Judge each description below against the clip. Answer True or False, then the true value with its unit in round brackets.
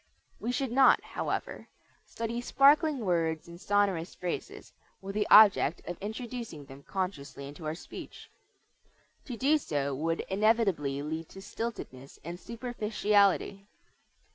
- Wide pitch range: True (6.2 semitones)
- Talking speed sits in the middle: False (125 wpm)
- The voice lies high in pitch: True (195 Hz)